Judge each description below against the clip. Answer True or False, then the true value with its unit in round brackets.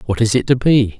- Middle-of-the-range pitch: False (115 Hz)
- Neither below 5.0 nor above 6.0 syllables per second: True (5.9 syllables/s)